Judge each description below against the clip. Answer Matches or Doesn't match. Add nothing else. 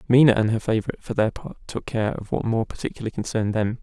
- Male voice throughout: Matches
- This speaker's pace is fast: Matches